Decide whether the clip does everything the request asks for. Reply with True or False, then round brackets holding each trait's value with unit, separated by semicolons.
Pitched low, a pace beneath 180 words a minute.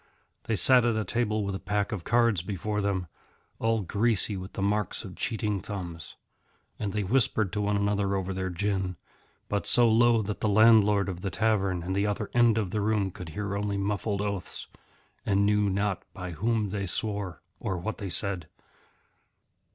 False (100 Hz; 185 wpm)